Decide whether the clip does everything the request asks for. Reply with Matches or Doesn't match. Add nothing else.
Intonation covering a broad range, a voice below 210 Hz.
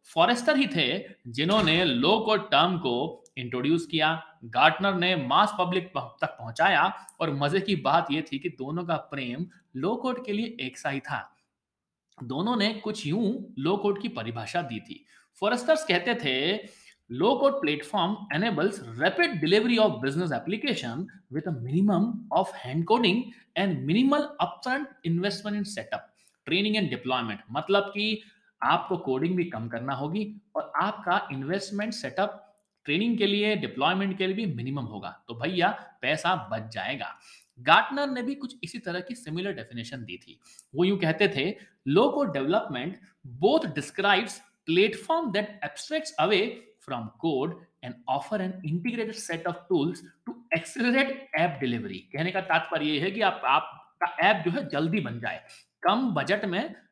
Matches